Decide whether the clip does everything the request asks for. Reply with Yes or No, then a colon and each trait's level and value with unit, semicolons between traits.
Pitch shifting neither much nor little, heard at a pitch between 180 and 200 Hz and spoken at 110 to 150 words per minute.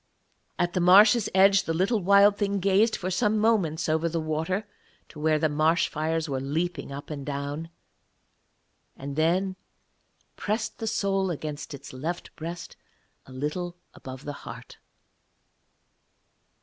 No: average, 4.4 semitones; medium, 170 Hz; average, 140 wpm